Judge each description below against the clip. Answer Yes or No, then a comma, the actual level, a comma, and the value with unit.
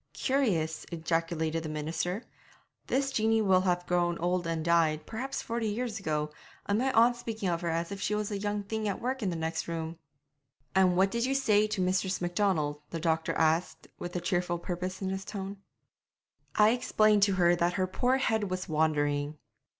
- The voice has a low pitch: No, medium, 185 Hz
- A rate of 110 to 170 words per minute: No, average, 190 wpm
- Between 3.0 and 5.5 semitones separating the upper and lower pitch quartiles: Yes, average, 4.2 semitones